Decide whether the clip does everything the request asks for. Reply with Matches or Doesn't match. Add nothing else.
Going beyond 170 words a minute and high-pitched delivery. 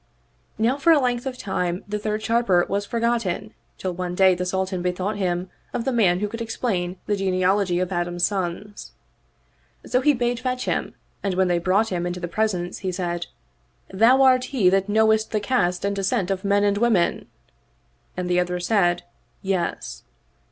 Matches